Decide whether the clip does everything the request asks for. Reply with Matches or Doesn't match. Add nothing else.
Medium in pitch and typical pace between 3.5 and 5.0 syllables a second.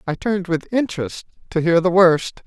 Doesn't match